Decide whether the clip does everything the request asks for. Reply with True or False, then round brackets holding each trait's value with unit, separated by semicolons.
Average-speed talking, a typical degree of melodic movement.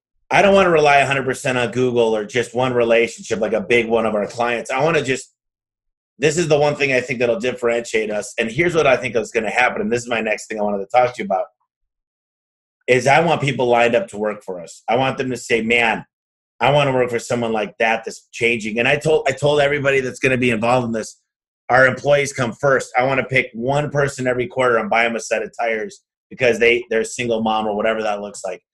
False (260 wpm; 3.1 semitones)